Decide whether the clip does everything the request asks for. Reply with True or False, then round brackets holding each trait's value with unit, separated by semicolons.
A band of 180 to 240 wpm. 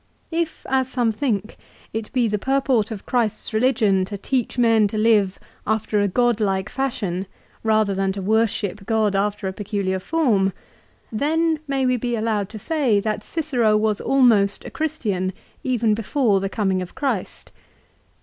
False (155 wpm)